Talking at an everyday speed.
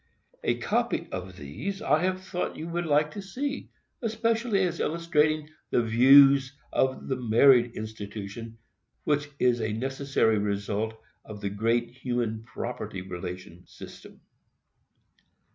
No: slow, 125 wpm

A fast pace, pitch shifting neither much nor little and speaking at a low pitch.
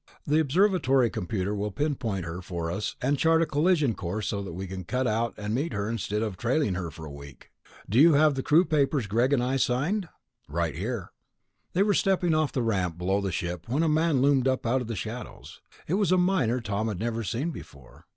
No: fast, 220 wpm; wide, 7.3 semitones; low, 120 Hz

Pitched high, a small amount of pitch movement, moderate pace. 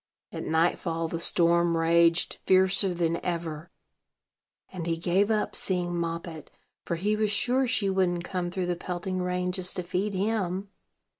No: medium, 180 Hz; narrow, 2.1 semitones; average, 155 wpm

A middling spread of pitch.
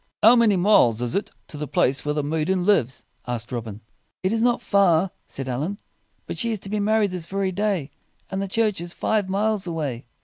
No: wide, 6.1 semitones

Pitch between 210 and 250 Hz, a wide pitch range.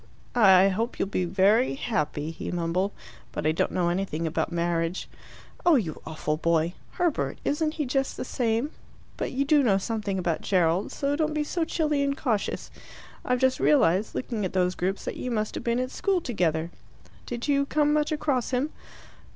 Yes: high, 220 Hz; wide, 8.0 semitones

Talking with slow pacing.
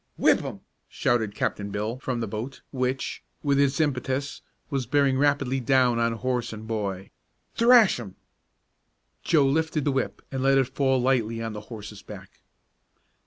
No: average, 160 wpm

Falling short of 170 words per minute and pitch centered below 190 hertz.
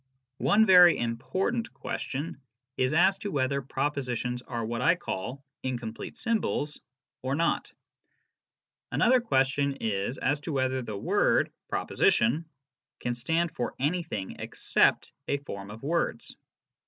Yes: average, 140 wpm; medium, 140 Hz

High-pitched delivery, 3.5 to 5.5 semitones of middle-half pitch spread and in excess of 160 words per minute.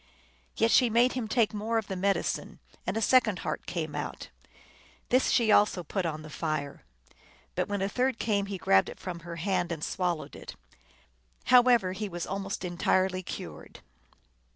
Yes: high, 195 Hz; average, 4.3 semitones; average, 175 wpm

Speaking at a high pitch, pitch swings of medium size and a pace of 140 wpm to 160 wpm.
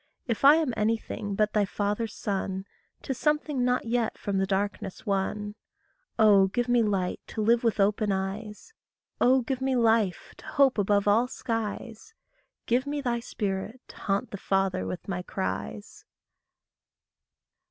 Yes: high, 215 Hz; average, 3.7 semitones; average, 155 wpm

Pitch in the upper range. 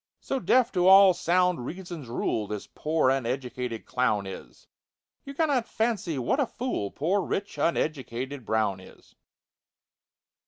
No: medium, 155 Hz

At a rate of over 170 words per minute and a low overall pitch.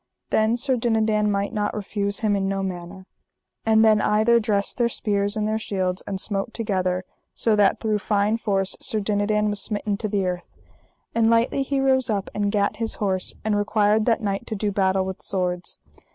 No: average, 195 wpm; high, 210 Hz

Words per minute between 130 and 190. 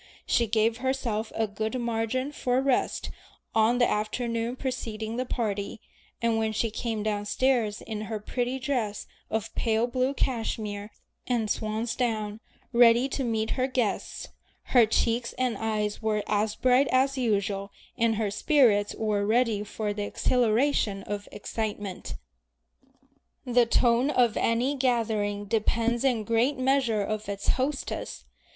Yes: average, 140 wpm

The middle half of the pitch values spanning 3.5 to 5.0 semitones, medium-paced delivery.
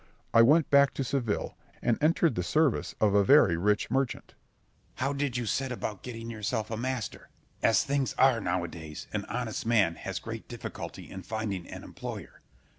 Yes: average, 4.5 semitones; average, 190 wpm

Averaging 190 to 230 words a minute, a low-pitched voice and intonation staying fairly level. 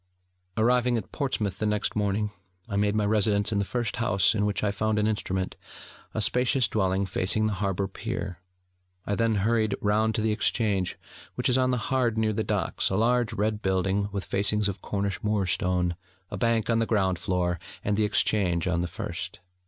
Yes: average, 195 wpm; low, 105 Hz; narrow, 2.2 semitones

